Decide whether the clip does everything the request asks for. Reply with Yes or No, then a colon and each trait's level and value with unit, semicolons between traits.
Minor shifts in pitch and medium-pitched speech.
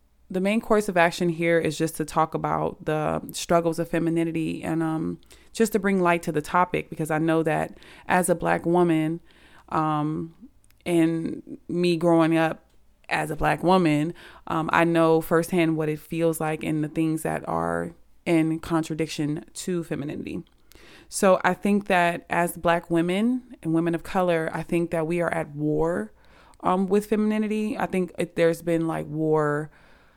Yes: narrow, 1.9 semitones; medium, 165 Hz